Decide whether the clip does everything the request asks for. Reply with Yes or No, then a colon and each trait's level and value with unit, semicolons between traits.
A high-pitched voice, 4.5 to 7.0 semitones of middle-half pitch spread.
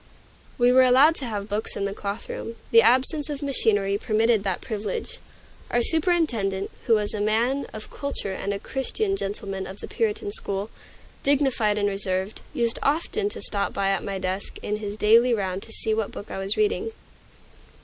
Yes: high, 220 Hz; average, 5.1 semitones